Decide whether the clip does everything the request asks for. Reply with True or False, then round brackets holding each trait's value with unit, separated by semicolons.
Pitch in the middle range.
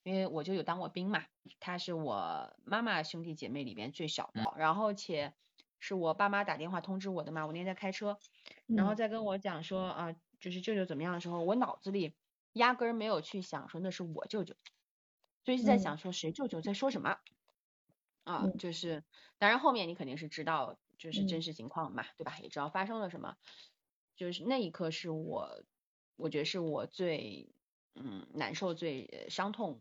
True (180 Hz)